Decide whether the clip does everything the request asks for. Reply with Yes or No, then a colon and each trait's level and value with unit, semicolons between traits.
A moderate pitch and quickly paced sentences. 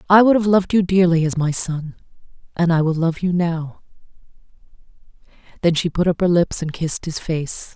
No: medium, 170 Hz; average, 195 wpm